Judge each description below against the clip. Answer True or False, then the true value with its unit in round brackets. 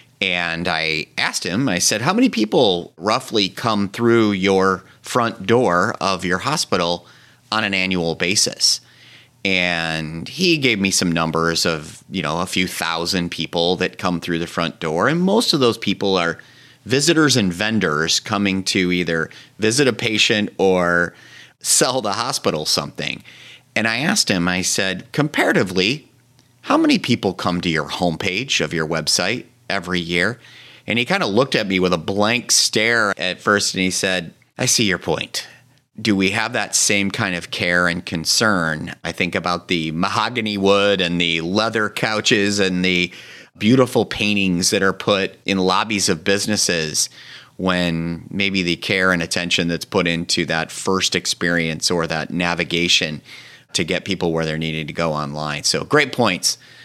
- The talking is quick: False (165 wpm)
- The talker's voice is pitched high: False (95 Hz)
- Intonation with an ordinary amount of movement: True (3.9 semitones)